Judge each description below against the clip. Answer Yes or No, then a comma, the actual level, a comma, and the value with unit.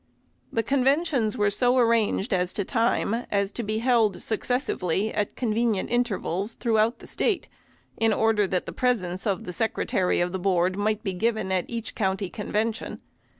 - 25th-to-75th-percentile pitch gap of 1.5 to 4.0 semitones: Yes, average, 3.3 semitones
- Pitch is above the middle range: Yes, high, 215 Hz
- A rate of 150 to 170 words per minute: Yes, average, 165 wpm